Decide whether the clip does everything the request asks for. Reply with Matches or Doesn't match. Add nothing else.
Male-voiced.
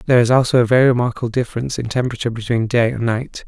Matches